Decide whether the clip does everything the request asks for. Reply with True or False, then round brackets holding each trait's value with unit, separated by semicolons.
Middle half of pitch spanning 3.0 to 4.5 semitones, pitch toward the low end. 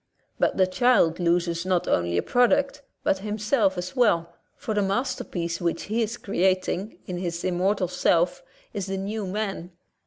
False (3.4 semitones; 190 Hz)